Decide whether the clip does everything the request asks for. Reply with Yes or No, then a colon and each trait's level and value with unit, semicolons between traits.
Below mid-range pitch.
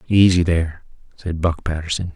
Yes: very low, 85 Hz